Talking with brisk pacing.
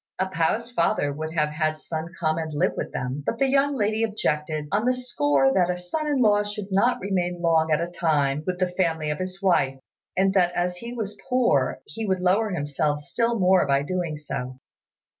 Yes: fast, 210 wpm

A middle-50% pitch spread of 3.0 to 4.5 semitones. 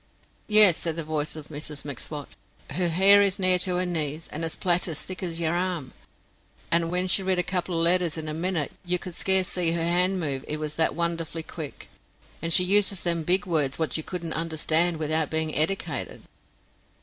No: narrow, 2.5 semitones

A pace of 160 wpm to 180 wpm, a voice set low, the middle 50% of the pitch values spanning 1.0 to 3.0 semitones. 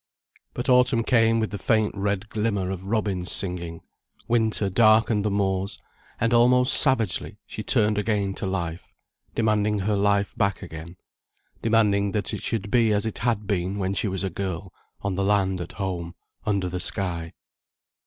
Yes: average, 165 wpm; low, 100 Hz; narrow, 2.6 semitones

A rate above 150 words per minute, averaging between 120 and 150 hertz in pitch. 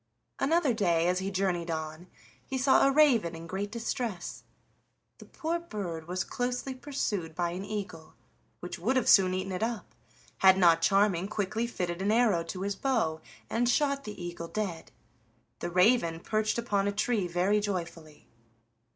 No: average, 165 wpm; high, 195 Hz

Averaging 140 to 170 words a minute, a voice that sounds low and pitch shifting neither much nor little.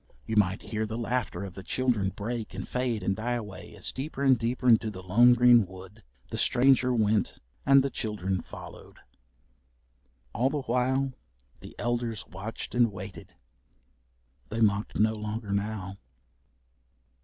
Yes: average, 150 wpm; low, 110 Hz; average, 3.4 semitones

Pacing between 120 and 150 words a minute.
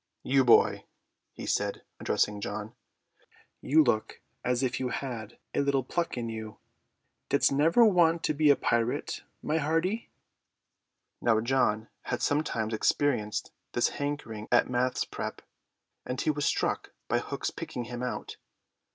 Yes: average, 145 wpm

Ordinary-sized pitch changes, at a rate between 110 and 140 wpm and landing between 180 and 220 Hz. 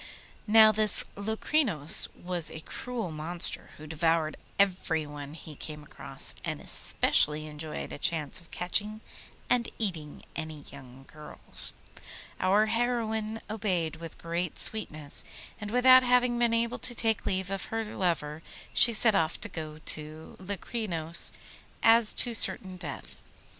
No: wide, 5.9 semitones; slow, 135 wpm; medium, 185 Hz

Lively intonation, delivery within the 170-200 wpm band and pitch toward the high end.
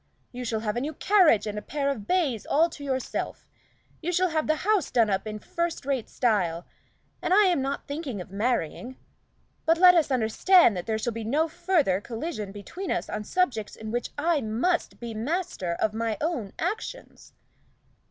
Yes: wide, 7.5 semitones; average, 190 wpm; very high, 260 Hz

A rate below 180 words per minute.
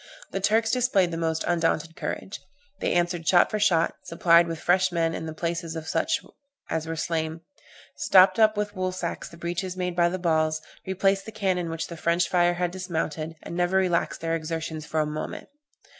No: average, 190 wpm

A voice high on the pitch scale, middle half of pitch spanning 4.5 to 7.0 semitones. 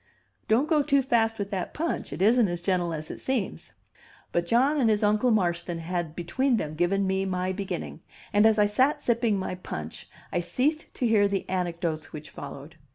Yes: high, 195 Hz; average, 5.2 semitones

